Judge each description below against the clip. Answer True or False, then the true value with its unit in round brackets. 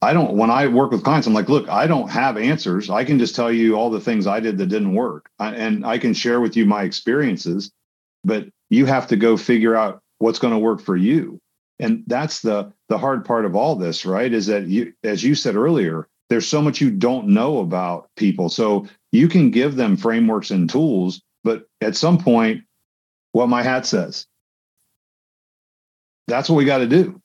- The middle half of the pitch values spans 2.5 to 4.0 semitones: False (4.7 semitones)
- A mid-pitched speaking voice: False (115 Hz)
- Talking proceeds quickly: True (215 wpm)